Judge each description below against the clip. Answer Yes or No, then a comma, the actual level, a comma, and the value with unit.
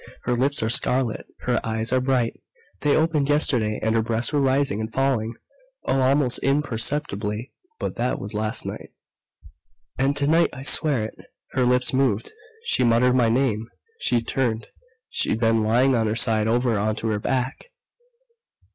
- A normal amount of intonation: Yes, average, 3.3 semitones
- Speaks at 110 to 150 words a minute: No, average, 160 wpm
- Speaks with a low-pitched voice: Yes, low, 125 Hz